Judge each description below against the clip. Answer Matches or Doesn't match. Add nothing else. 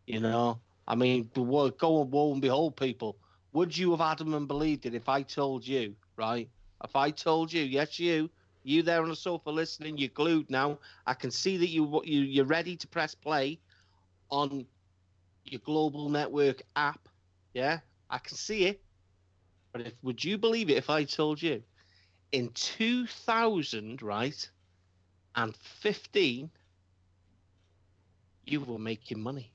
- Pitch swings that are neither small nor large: Doesn't match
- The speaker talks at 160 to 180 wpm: Matches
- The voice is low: Matches